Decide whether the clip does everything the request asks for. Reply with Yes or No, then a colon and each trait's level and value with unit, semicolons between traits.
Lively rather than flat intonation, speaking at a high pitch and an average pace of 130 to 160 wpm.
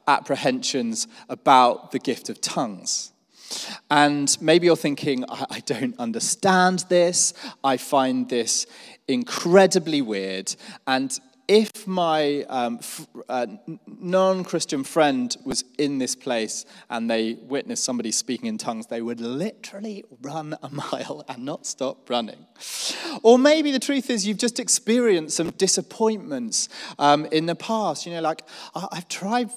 No: wide, 8.6 semitones; medium, 170 Hz; average, 140 wpm